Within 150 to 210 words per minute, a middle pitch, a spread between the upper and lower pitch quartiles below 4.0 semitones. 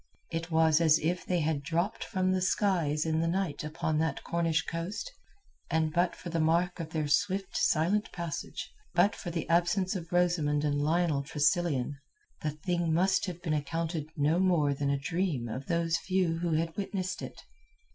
Yes: average, 180 wpm; medium, 165 Hz; narrow, 2.5 semitones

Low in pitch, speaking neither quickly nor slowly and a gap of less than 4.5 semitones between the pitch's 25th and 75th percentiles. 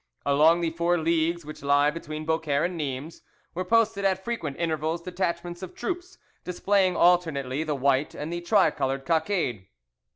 No: medium, 165 Hz; average, 155 wpm; average, 3.3 semitones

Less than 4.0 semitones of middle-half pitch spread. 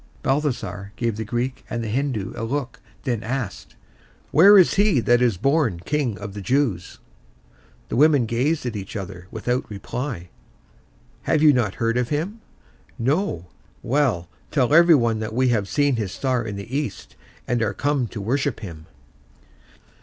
No: average, 5.2 semitones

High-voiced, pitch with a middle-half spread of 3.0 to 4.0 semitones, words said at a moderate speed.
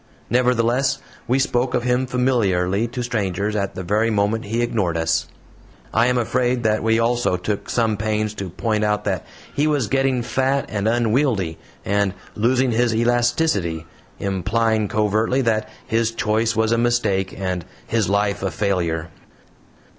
No: low, 110 Hz; average, 3.3 semitones; average, 155 wpm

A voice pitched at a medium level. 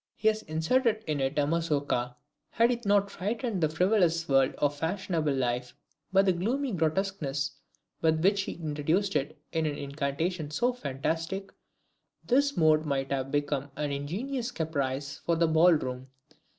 Yes: medium, 160 Hz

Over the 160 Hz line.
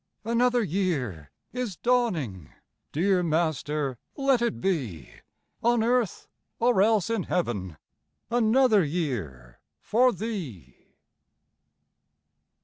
Yes: medium, 185 Hz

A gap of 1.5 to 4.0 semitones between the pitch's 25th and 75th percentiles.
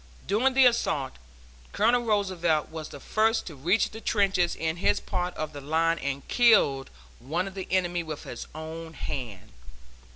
No: average, 5.0 semitones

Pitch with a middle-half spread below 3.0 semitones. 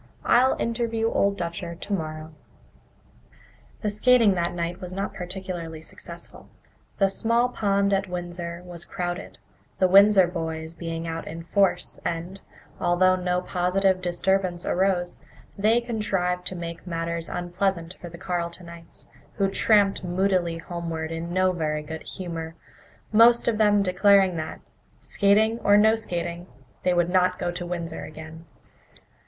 Yes: narrow, 2.6 semitones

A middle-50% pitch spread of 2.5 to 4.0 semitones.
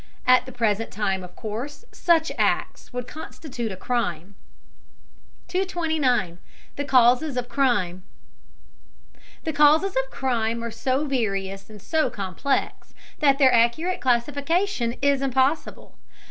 No: average, 4.6 semitones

